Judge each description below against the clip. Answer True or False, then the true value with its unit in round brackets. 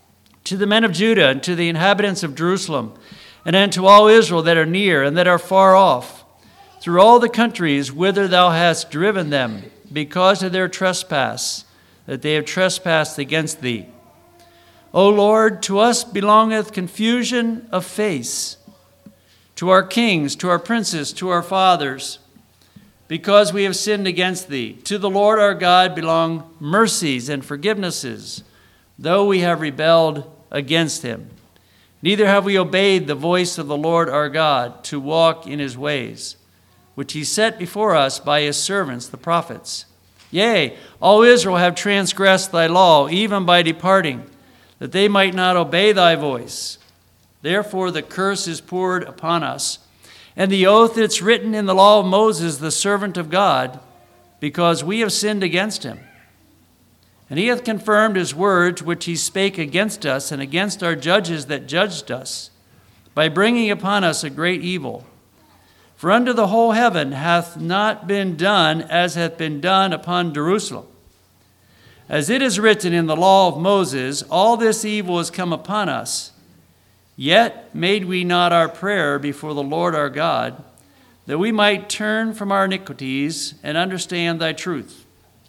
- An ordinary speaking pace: True (160 wpm)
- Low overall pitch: False (175 Hz)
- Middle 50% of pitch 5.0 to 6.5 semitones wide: True (5.3 semitones)